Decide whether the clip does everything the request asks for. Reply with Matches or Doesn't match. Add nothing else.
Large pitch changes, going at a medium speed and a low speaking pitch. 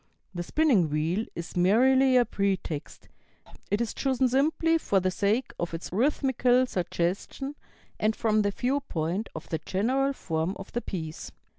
Doesn't match